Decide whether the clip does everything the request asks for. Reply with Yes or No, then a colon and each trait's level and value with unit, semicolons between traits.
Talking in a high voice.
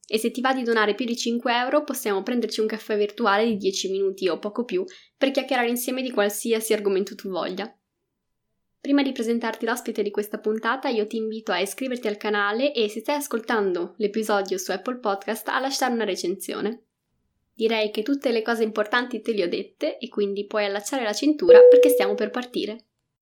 Yes: high, 225 Hz